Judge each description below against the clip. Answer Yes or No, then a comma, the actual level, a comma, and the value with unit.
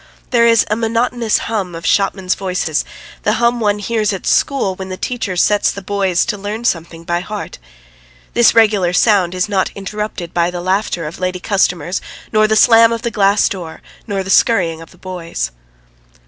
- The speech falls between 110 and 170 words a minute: No, average, 185 wpm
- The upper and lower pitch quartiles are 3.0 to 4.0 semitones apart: Yes, average, 3.4 semitones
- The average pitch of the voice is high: Yes, high, 195 Hz